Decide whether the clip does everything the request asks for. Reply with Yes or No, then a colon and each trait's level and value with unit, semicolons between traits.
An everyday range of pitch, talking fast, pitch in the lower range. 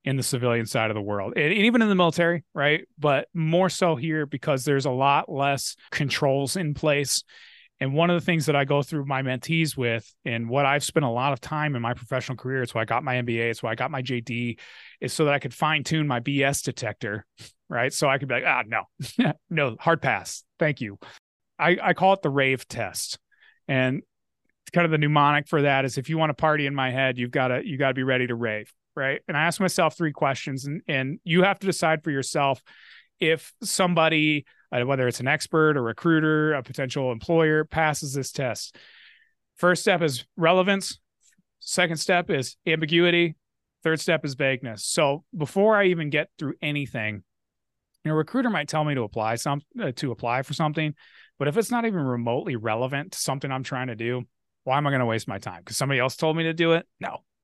No: average, 3.9 semitones; fast, 215 wpm; medium, 145 Hz